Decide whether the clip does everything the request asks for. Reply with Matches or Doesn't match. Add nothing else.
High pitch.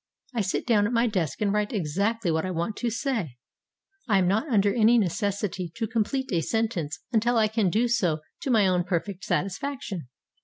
Matches